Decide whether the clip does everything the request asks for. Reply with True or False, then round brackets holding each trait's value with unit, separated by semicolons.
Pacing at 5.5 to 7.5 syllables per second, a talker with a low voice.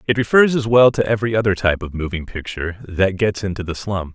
True (6.4 syllables/s; 100 Hz)